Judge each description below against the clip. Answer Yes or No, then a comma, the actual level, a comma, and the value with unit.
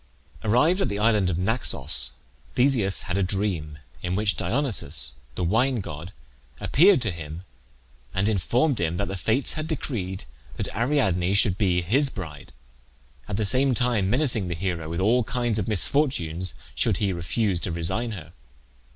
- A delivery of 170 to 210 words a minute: No, average, 160 wpm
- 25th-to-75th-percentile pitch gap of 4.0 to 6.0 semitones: Yes, wide, 5.6 semitones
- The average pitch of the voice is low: Yes, low, 100 Hz